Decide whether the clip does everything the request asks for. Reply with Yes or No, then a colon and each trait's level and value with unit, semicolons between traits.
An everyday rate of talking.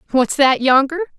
Yes: average, 150 wpm